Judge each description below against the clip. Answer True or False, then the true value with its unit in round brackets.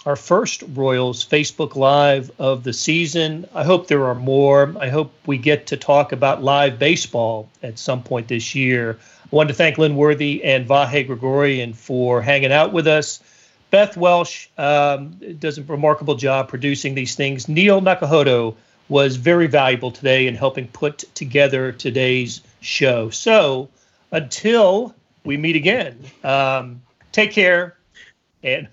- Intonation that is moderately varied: True (3.1 semitones)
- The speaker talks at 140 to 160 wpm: True (150 wpm)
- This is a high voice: False (140 Hz)